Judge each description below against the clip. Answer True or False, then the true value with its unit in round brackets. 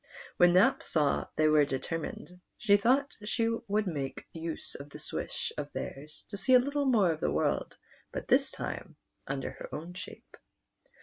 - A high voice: False (175 Hz)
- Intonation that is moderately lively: False (6.2 semitones)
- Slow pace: False (180 wpm)